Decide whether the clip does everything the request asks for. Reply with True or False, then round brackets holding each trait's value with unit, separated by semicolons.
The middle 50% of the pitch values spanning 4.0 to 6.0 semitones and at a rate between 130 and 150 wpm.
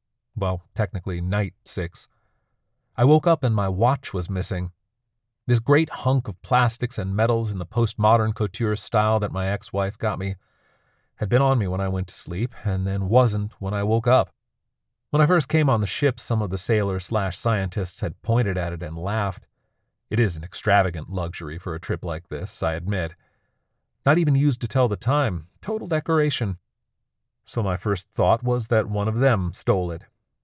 False (4.3 semitones; 190 wpm)